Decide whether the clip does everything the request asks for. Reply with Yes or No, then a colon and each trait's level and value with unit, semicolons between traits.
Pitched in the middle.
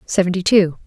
Yes: medium, 180 Hz